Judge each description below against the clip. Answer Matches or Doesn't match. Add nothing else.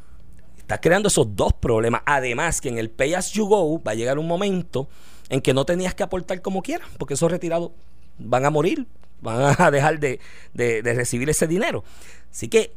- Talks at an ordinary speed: Doesn't match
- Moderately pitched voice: Matches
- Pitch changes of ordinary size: Doesn't match